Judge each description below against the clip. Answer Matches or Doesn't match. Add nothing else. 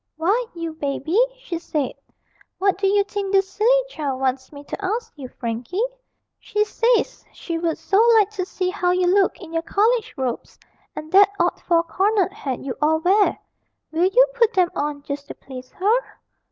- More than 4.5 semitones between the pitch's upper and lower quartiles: Matches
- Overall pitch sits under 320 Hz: Doesn't match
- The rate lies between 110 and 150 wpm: Doesn't match